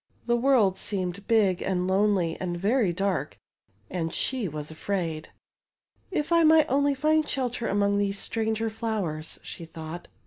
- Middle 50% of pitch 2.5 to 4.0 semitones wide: No, average, 5.2 semitones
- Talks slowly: No, average, 145 wpm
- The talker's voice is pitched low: No, high, 200 Hz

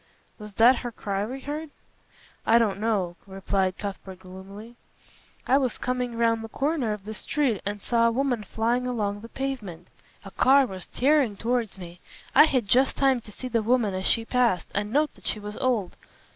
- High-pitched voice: Yes, high, 230 Hz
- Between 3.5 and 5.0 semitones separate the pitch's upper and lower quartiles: Yes, average, 3.9 semitones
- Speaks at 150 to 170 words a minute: No, average, 190 wpm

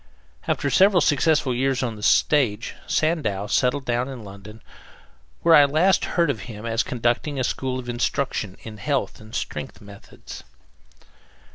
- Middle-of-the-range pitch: No, low, 125 Hz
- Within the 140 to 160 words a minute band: Yes, average, 150 wpm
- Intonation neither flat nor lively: Yes, average, 4.8 semitones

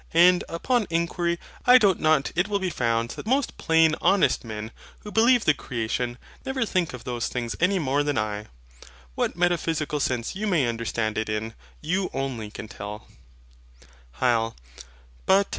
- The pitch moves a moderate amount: No, wide, 7.8 semitones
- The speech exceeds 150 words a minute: Yes, average, 160 wpm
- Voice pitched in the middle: Yes, medium, 150 Hz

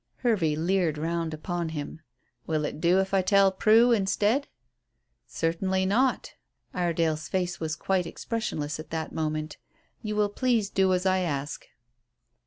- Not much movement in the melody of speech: No, average, 3.7 semitones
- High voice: No, medium, 180 Hz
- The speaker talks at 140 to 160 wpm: Yes, average, 145 wpm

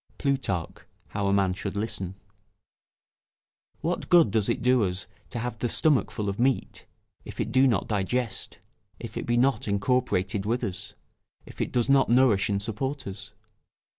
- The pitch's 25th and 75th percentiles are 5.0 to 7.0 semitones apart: No, average, 4.4 semitones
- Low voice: Yes, low, 115 Hz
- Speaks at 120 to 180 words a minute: Yes, average, 165 wpm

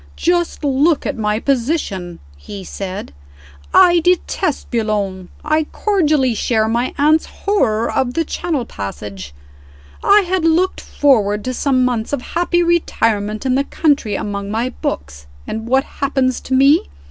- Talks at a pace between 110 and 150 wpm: Yes, average, 145 wpm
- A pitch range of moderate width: No, wide, 6.8 semitones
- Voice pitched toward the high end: Yes, very high, 255 Hz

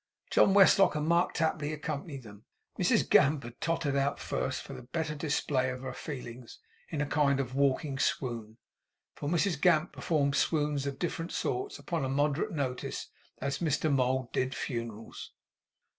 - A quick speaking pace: No, average, 160 wpm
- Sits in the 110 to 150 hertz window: Yes, medium, 140 Hz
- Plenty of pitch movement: No, average, 3.3 semitones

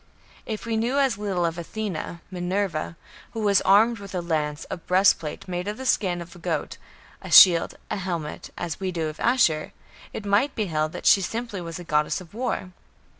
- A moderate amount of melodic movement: Yes, average, 3.9 semitones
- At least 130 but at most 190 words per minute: No, average, 200 wpm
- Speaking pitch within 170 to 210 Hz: Yes, medium, 185 Hz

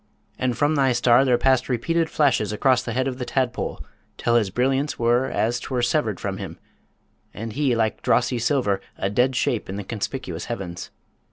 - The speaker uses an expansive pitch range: No, average, 2.7 semitones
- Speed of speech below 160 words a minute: No, average, 185 wpm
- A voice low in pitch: Yes, low, 125 Hz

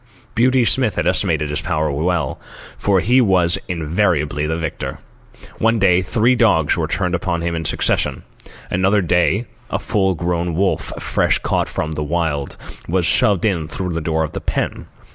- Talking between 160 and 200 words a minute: Yes, average, 175 wpm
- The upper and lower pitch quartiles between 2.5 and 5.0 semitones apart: Yes, average, 3.6 semitones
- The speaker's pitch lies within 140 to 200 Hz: No, very low, 90 Hz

